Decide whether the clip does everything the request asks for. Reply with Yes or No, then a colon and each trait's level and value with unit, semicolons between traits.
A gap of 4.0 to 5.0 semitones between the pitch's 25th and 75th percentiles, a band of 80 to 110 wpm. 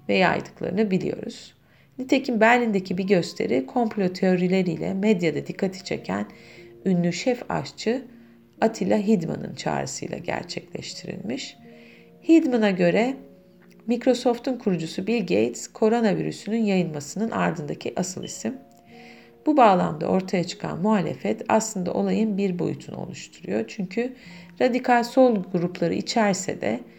Yes: average, 4.7 semitones; average, 100 wpm